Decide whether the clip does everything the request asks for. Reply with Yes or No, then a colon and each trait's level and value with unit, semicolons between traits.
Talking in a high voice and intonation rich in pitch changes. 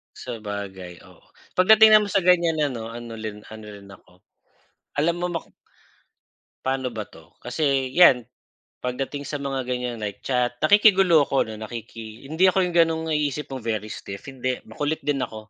No: low, 130 Hz; wide, 6.4 semitones